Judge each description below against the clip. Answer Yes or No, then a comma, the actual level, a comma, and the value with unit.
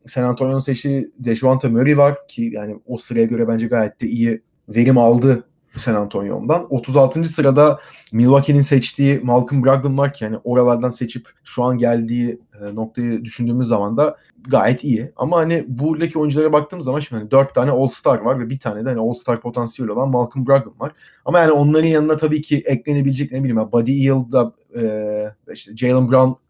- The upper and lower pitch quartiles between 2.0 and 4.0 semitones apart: Yes, average, 2.9 semitones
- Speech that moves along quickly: Yes, fast, 175 wpm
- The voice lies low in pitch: Yes, low, 130 Hz